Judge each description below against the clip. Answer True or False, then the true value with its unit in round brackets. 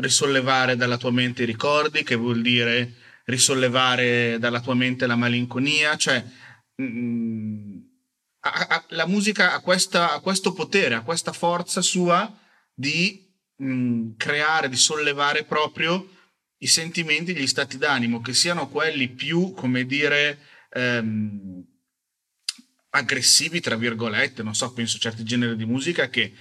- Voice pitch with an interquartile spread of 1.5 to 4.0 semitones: False (5.5 semitones)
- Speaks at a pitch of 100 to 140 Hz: True (135 Hz)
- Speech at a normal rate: True (135 wpm)